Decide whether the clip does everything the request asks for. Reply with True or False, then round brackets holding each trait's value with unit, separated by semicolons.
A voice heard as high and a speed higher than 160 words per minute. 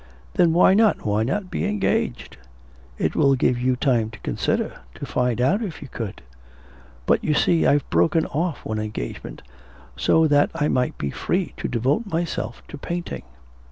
False (145 Hz; 170 wpm)